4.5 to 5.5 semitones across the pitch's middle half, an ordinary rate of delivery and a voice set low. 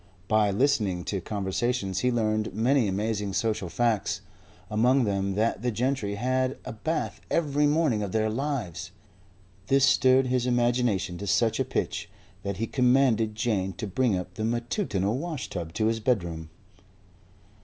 No: average, 4.1 semitones; average, 150 wpm; low, 110 Hz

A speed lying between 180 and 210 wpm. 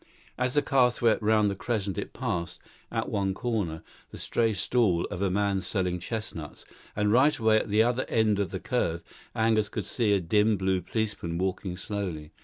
Yes: average, 190 wpm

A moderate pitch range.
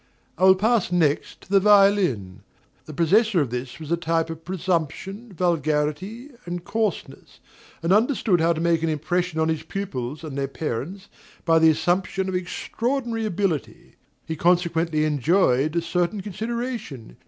Yes: average, 3.9 semitones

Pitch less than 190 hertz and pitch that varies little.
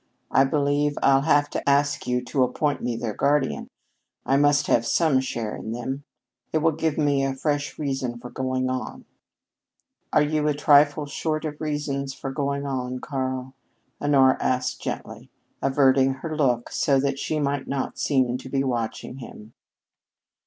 Yes: low, 135 Hz; narrow, 2.1 semitones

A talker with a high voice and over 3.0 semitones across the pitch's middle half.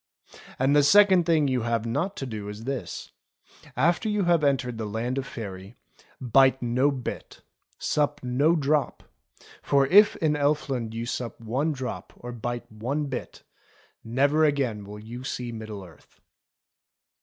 No: low, 130 Hz; average, 4.2 semitones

